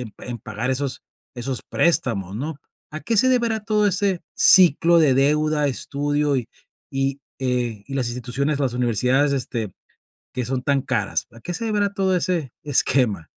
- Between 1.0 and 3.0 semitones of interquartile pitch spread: No, average, 5.3 semitones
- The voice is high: No, medium, 140 Hz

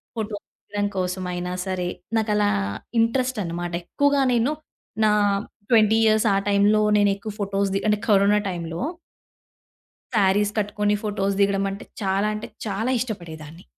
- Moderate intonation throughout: No, narrow, 2.0 semitones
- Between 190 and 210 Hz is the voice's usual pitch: Yes, high, 205 Hz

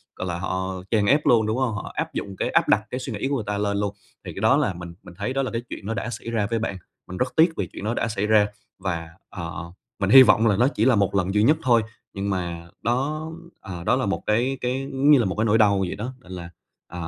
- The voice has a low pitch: Yes, low, 105 Hz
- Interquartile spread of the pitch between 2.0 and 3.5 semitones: No, average, 4.4 semitones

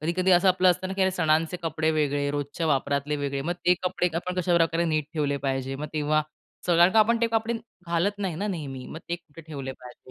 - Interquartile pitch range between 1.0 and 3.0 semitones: No, average, 3.7 semitones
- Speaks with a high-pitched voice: No, medium, 160 Hz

